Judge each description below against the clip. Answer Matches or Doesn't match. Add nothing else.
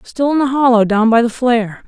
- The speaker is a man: Doesn't match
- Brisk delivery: Matches